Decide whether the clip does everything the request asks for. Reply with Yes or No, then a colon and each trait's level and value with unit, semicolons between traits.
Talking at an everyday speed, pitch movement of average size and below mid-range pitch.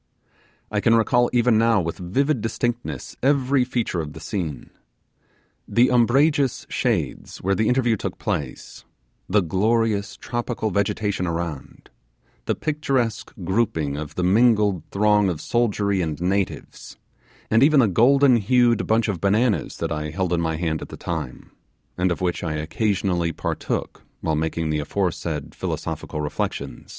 No: average, 145 wpm; wide, 6.0 semitones; low, 100 Hz